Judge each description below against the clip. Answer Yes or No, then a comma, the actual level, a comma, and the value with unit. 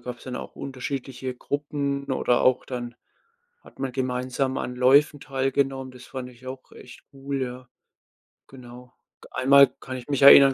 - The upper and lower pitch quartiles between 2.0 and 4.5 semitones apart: No, narrow, 1.5 semitones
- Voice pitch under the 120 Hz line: No, low, 130 Hz